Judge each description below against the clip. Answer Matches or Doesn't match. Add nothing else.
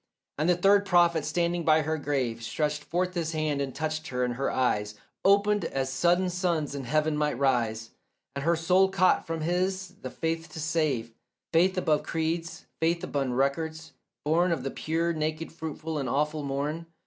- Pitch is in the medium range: Matches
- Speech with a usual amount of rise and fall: Matches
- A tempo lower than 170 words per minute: Doesn't match